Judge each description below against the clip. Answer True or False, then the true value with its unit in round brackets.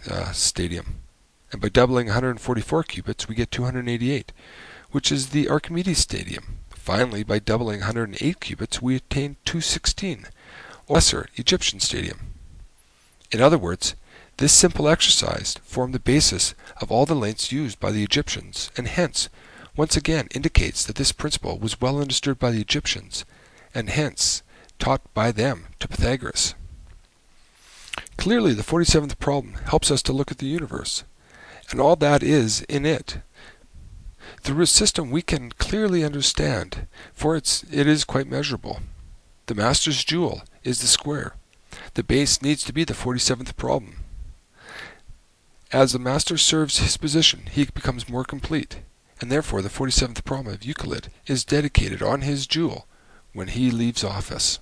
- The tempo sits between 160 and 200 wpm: False (150 wpm)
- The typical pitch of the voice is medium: False (130 Hz)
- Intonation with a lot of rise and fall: True (5.7 semitones)